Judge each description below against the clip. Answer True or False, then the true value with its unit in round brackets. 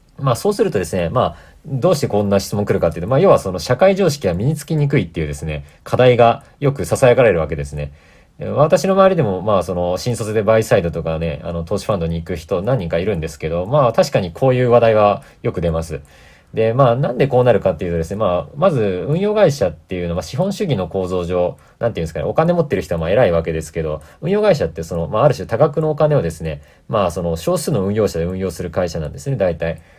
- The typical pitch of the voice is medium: False (100 Hz)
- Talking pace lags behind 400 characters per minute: False (490 characters per minute)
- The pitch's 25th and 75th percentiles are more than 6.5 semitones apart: True (9.0 semitones)